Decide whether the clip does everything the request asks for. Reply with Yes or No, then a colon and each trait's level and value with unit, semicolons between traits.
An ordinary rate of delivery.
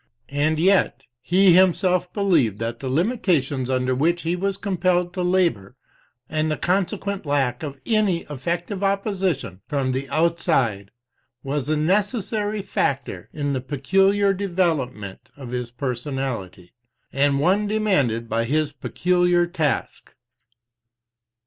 No: slow, 125 wpm